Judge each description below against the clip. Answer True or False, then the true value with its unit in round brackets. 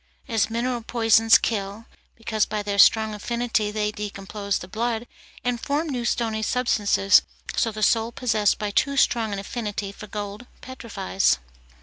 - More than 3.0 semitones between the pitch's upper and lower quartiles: False (2.4 semitones)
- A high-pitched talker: True (220 Hz)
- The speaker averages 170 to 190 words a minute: False (150 wpm)